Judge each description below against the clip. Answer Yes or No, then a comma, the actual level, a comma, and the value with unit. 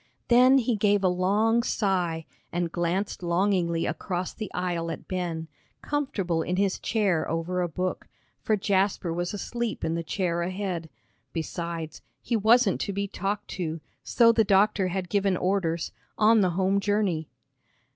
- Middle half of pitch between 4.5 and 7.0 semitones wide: No, average, 3.3 semitones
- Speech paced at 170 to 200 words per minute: No, average, 155 wpm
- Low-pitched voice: No, medium, 185 Hz